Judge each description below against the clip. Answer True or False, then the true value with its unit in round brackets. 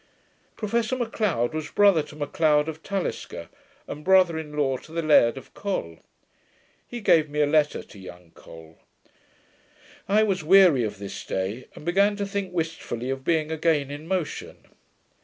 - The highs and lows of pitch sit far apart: True (6.1 semitones)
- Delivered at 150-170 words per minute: True (160 wpm)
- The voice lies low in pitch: False (155 Hz)